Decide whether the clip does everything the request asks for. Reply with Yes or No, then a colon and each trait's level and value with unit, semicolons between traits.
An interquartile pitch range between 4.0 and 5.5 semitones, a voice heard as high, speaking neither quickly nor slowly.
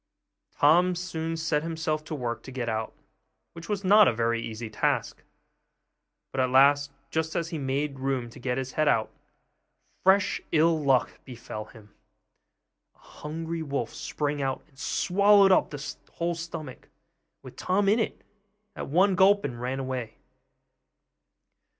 No: average, 4.5 semitones; medium, 150 Hz; average, 155 wpm